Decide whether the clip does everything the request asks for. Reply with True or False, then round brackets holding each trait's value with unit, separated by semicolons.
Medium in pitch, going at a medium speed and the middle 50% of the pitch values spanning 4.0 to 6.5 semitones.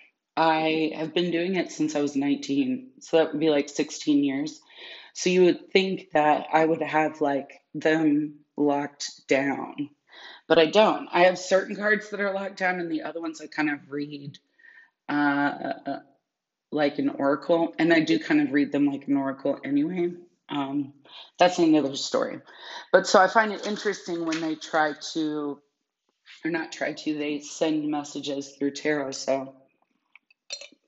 True (160 Hz; 165 wpm; 5.0 semitones)